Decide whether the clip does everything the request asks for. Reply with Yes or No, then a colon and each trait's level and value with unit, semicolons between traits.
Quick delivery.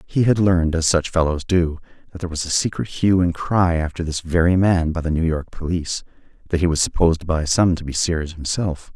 Yes: fast, 230 wpm